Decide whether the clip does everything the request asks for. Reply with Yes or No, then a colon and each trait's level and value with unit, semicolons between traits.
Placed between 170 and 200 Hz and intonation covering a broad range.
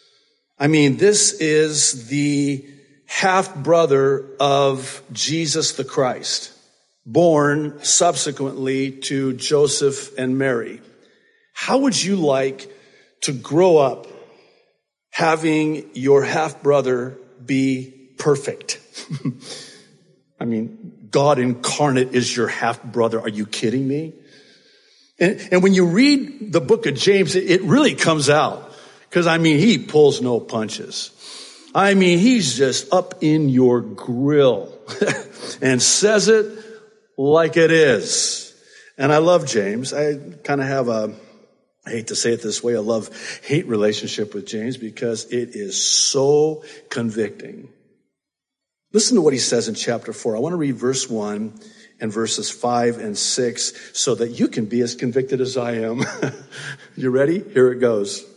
No: medium, 145 Hz; wide, 6.5 semitones